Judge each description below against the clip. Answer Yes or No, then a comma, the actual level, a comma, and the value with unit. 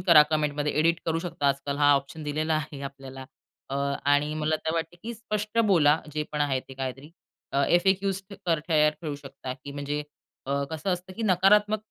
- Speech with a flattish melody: No, average, 3.7 semitones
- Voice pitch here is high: No, medium, 150 Hz